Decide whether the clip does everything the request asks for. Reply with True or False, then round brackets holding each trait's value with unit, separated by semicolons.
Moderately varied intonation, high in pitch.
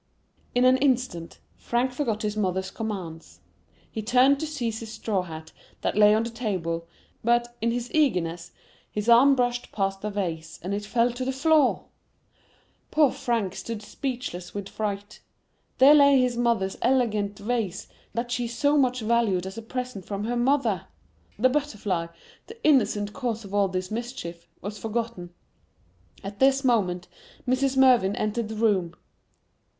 True (4.2 semitones; 225 Hz)